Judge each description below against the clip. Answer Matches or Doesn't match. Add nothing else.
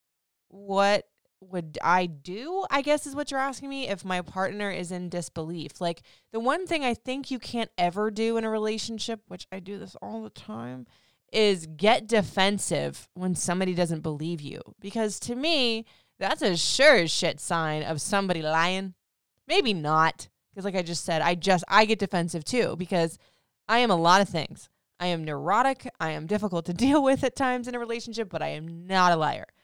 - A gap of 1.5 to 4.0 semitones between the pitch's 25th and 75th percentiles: Doesn't match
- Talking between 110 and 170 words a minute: Doesn't match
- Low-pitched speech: Doesn't match